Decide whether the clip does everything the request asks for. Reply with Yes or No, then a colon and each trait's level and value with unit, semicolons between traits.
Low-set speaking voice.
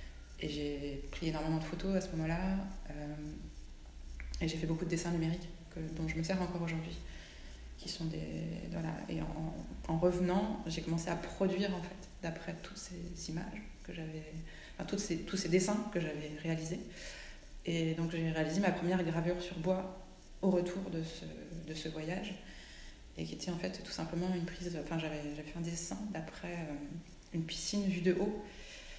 No: medium, 170 Hz